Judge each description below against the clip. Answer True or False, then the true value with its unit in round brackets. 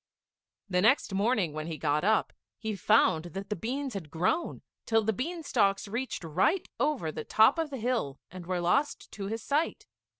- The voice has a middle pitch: False (210 Hz)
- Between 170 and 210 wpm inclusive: True (190 wpm)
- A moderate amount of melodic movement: False (6.6 semitones)